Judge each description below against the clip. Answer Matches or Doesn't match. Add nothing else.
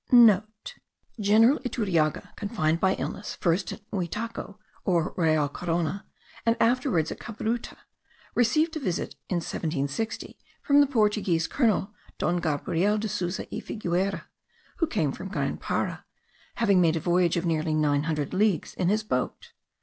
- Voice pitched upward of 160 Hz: Matches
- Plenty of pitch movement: Doesn't match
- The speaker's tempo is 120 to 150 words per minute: Matches